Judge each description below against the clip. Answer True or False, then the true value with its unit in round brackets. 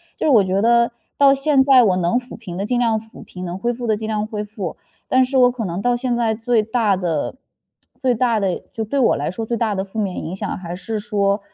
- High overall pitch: True (220 Hz)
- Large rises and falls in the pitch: False (3.7 semitones)